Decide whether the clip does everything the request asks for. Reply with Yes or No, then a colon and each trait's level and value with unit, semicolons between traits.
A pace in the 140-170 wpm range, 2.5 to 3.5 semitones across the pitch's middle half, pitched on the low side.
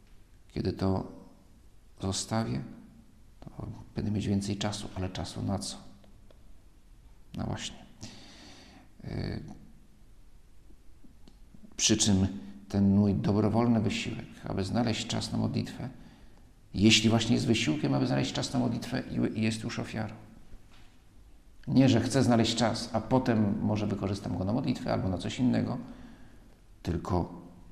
No: average, 120 wpm; average, 2.8 semitones; low, 110 Hz